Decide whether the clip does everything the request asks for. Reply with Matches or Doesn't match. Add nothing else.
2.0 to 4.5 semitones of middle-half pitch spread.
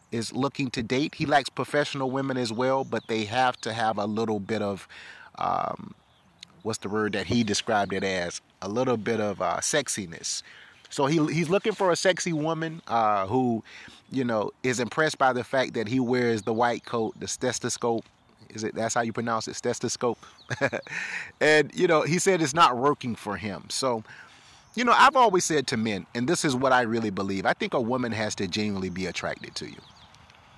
Matches